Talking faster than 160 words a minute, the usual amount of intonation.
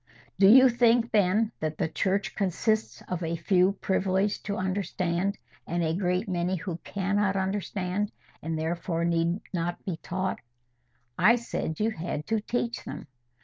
No: average, 150 wpm; average, 3.2 semitones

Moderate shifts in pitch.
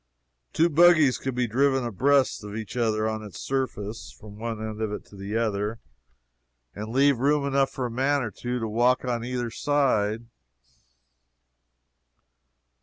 Yes: average, 3.6 semitones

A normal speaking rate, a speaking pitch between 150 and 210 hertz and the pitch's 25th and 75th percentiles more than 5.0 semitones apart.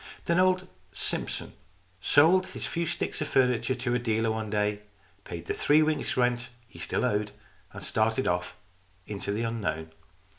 No: average, 160 wpm; low, 120 Hz; wide, 5.6 semitones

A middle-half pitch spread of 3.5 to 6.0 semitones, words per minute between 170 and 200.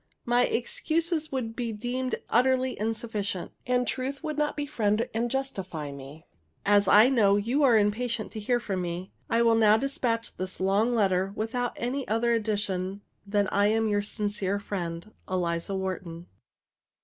No: average, 3.9 semitones; average, 160 wpm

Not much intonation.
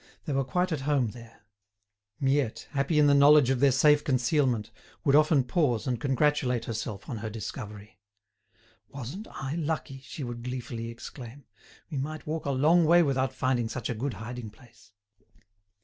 No: average, 3.7 semitones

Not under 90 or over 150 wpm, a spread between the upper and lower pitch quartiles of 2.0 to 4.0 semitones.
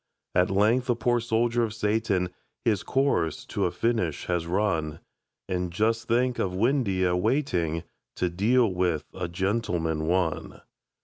No: average, 140 wpm; average, 4.7 semitones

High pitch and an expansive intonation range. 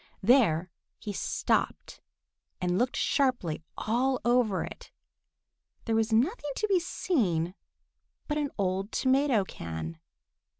Yes: high, 225 Hz; wide, 6.5 semitones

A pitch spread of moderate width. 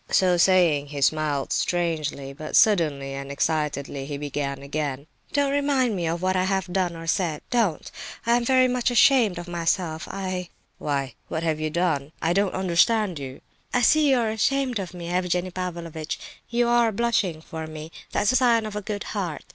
No: wide, 5.7 semitones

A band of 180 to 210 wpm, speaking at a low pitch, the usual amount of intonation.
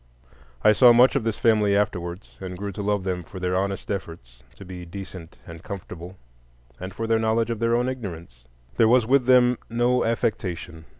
Yes: average, 190 wpm; low, 100 Hz; average, 4.4 semitones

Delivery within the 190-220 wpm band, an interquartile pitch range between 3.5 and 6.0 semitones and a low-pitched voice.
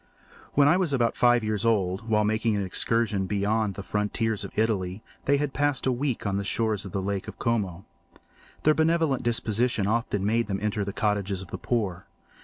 No: average, 195 wpm; average, 2.9 semitones; low, 110 Hz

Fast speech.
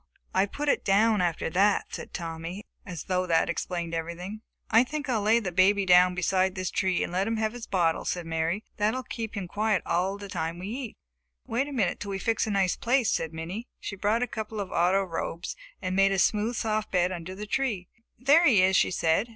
Yes: fast, 230 wpm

